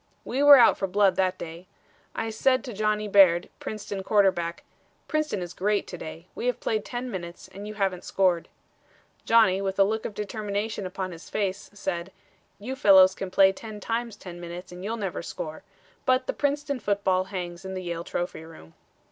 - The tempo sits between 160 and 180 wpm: No, average, 190 wpm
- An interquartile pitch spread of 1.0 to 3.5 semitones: Yes, average, 3.1 semitones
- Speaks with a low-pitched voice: No, high, 195 Hz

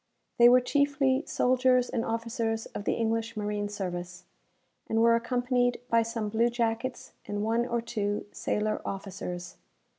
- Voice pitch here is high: Yes, high, 230 Hz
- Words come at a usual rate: Yes, average, 145 wpm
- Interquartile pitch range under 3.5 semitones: Yes, average, 2.8 semitones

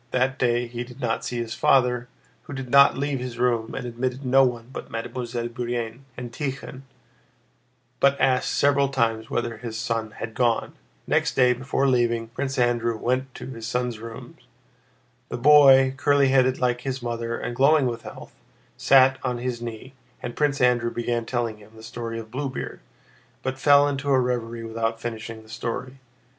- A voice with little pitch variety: Yes, narrow, 2.2 semitones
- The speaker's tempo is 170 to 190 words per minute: Yes, average, 175 wpm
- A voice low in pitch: Yes, low, 125 Hz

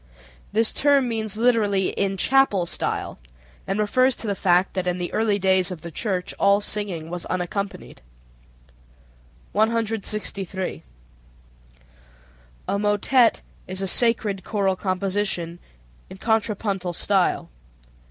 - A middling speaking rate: No, slow, 115 wpm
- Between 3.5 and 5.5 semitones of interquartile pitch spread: No, average, 2.7 semitones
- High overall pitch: Yes, high, 200 Hz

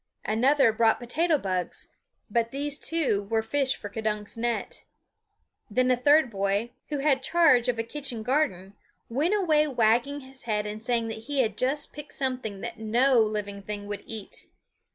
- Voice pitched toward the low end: No, high, 235 Hz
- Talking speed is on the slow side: No, average, 170 wpm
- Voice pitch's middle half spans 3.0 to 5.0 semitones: Yes, average, 4.5 semitones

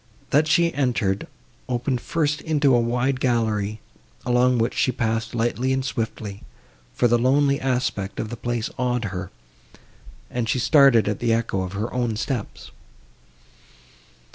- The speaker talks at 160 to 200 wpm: No, average, 145 wpm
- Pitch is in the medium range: No, low, 120 Hz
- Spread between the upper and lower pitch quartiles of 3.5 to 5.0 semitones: No, average, 2.8 semitones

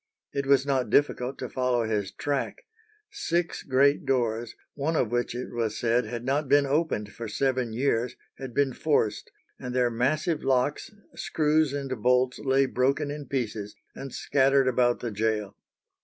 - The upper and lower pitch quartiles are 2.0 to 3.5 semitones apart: Yes, average, 2.9 semitones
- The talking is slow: No, average, 160 wpm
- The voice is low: Yes, low, 130 Hz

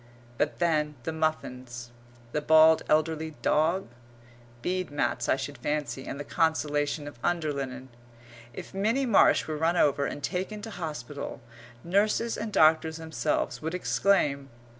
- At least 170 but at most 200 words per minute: No, average, 140 wpm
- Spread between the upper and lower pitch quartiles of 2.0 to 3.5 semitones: Yes, average, 3.1 semitones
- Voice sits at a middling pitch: Yes, medium, 155 Hz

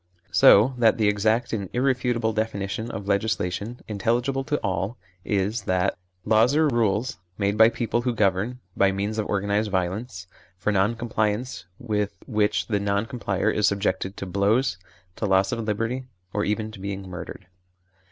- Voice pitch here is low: Yes, low, 105 Hz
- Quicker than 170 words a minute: No, average, 160 wpm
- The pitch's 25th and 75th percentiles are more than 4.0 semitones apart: No, average, 2.9 semitones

